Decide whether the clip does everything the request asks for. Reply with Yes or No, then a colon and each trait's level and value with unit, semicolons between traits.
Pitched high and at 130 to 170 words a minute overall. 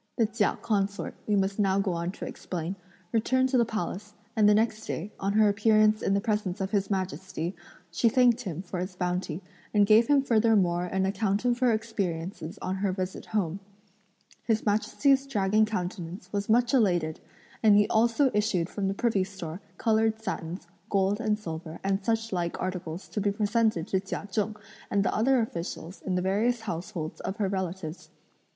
No: high, 200 Hz; average, 185 wpm